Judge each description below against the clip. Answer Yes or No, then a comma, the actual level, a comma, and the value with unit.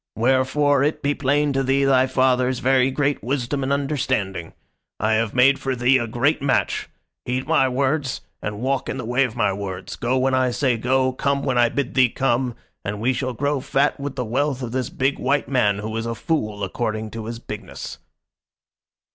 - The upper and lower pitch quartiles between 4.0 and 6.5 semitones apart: No, average, 2.8 semitones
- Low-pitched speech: Yes, low, 130 Hz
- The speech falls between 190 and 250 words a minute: Yes, average, 200 wpm